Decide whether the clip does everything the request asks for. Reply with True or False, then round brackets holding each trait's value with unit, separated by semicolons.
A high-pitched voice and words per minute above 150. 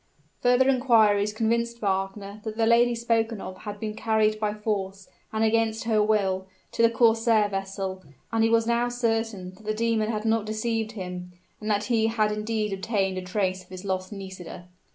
True (215 Hz; 185 wpm)